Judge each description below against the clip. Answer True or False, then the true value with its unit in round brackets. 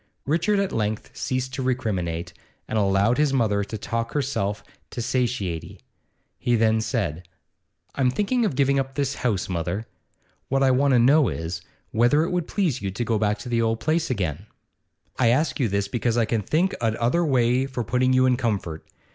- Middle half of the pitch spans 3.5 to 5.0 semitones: True (4.3 semitones)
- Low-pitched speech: True (120 Hz)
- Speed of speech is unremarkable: True (190 wpm)